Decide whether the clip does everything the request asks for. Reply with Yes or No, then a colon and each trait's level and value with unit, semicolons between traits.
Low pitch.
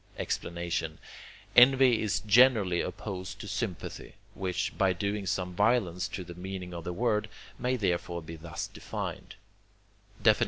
Yes: very low, 95 Hz